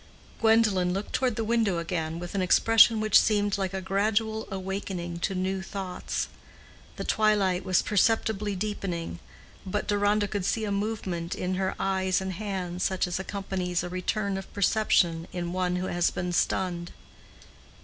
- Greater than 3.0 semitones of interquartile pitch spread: No, narrow, 2.5 semitones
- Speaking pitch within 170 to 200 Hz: Yes, high, 190 Hz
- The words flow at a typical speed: Yes, average, 160 wpm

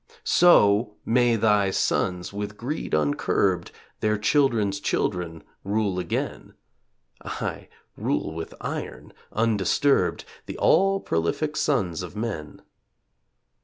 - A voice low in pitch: Yes, low, 105 Hz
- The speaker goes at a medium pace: No, slow, 100 wpm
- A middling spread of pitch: Yes, average, 4.7 semitones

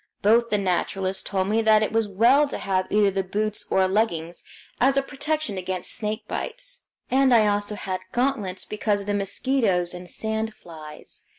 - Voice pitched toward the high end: Yes, high, 210 Hz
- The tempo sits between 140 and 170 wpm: No, average, 180 wpm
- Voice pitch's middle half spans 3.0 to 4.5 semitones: Yes, average, 3.6 semitones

